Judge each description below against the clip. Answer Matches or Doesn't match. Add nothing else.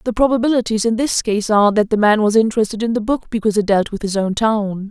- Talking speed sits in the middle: Doesn't match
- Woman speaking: Matches